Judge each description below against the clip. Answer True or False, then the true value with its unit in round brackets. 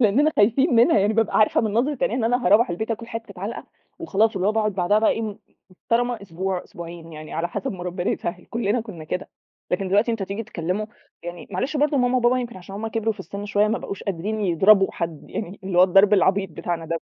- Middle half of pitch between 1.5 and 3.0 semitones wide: False (3.9 semitones)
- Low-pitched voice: False (205 Hz)